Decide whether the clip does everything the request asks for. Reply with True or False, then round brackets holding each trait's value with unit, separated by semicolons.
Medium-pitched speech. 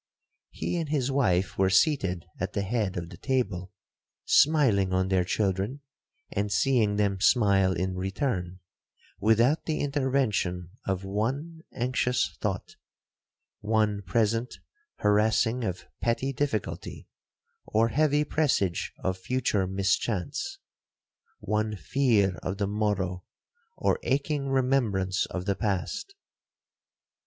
False (105 Hz)